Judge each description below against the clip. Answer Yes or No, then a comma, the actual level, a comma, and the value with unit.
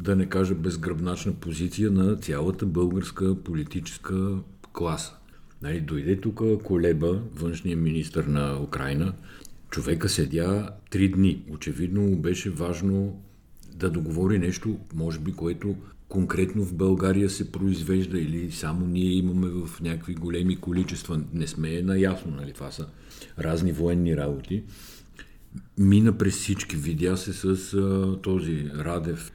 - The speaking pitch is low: Yes, very low, 90 Hz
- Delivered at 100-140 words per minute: Yes, average, 125 wpm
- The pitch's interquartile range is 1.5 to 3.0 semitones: Yes, narrow, 2.6 semitones